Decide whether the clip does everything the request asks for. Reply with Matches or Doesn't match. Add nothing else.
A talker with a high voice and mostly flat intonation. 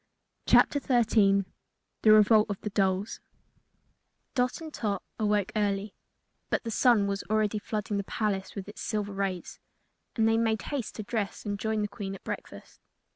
Matches